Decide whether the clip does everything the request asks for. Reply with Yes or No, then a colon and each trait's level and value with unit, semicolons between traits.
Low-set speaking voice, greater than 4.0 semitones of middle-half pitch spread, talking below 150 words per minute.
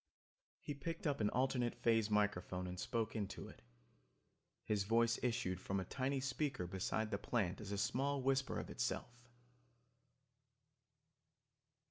Yes: low, 115 Hz; average, 4.7 semitones; slow, 135 wpm